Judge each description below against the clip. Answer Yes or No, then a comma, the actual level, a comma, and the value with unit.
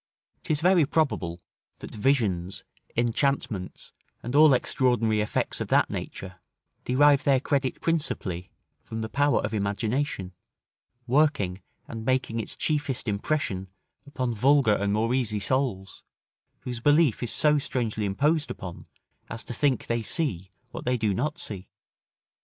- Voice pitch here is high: No, low, 120 Hz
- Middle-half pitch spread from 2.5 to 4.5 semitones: No, wide, 5.5 semitones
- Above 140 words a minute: No, slow, 135 wpm